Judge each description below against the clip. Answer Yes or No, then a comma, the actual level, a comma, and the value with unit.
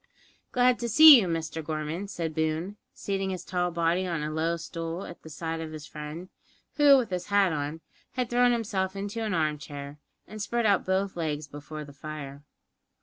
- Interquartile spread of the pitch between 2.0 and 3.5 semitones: No, average, 4.5 semitones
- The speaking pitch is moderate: Yes, medium, 170 Hz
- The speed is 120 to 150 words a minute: No, average, 190 wpm